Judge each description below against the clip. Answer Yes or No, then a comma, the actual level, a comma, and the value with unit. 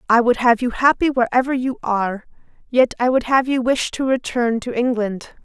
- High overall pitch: Yes, high, 245 Hz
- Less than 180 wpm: No, average, 200 wpm